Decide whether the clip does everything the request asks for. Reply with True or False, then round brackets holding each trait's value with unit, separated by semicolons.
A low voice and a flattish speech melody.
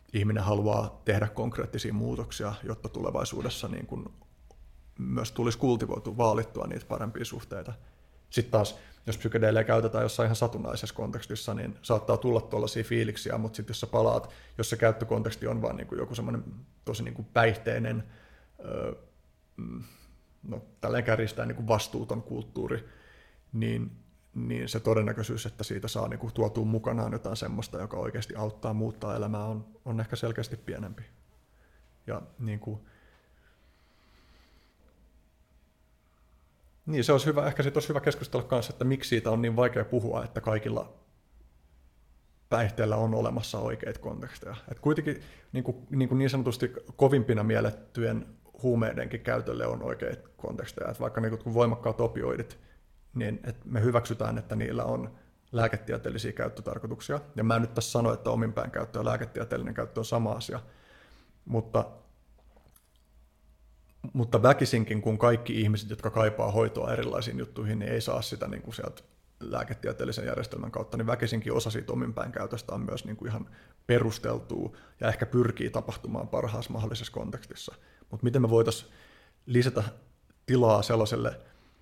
True (110 Hz; 2.1 semitones)